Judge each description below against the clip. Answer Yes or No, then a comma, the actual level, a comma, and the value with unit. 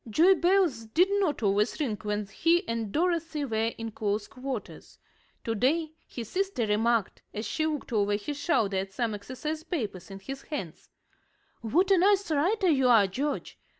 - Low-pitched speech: No, very high, 250 Hz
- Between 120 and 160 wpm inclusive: No, average, 170 wpm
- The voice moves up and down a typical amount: No, wide, 7.5 semitones